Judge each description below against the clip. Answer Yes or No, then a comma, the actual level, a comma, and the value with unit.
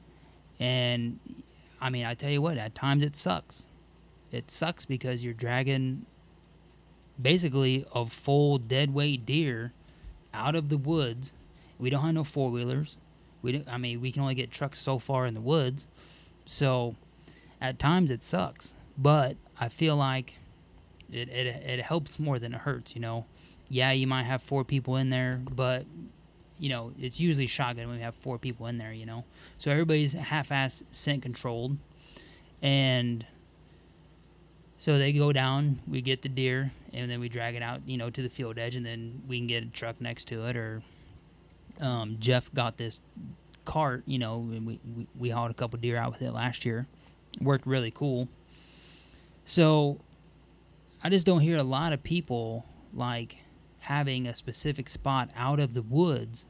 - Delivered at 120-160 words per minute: No, average, 175 wpm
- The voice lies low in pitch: Yes, low, 130 Hz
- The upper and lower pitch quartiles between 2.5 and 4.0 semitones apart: Yes, average, 3.1 semitones